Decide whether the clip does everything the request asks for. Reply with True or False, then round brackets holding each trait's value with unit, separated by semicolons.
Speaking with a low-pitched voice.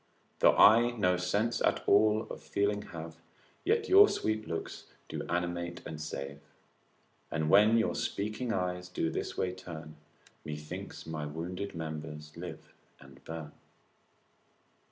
True (90 Hz)